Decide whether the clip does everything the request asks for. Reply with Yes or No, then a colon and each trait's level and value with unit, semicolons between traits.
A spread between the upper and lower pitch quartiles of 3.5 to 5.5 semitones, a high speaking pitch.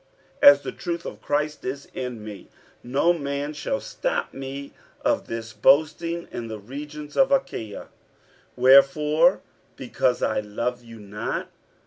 No: average, 4.1 semitones; medium, 140 Hz